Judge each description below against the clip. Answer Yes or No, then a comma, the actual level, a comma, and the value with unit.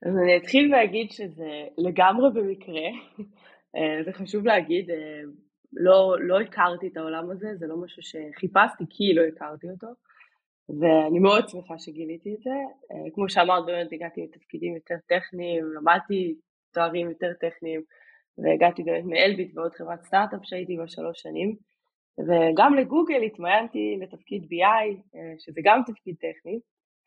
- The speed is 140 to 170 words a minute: No, average, 130 wpm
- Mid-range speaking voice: Yes, medium, 180 Hz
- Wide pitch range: No, average, 3.7 semitones